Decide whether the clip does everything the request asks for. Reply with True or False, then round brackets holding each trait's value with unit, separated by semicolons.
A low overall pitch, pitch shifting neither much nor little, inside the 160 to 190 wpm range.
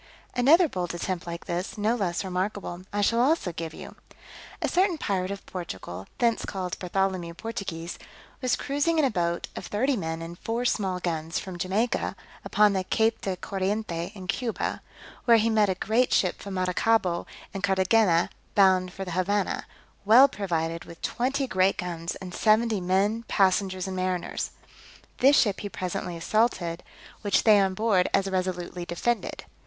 False (190 Hz; 3.7 semitones; 165 wpm)